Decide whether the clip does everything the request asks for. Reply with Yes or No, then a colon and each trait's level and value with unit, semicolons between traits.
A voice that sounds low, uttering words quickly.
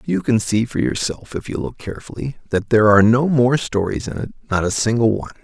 Yes: low, 110 Hz; fast, 230 wpm